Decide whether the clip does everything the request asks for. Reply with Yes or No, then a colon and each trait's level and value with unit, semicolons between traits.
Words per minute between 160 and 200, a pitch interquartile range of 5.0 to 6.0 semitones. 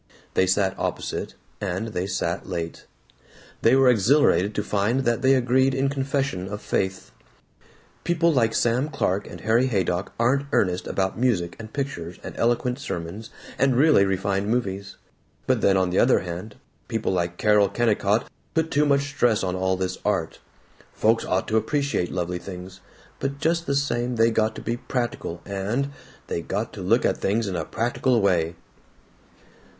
Yes: average, 165 wpm; average, 5.3 semitones